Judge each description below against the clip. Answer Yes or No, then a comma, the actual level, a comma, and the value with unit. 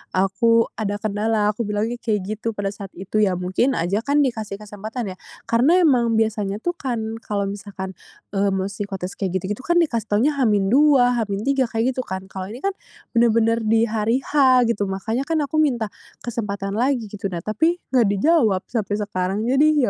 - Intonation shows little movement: No, average, 3.4 semitones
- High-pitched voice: Yes, high, 220 Hz